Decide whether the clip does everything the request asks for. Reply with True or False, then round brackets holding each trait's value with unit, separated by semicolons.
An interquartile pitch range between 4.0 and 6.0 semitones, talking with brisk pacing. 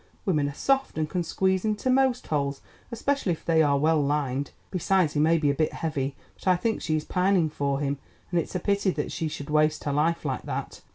True (4.5 semitones; 230 wpm)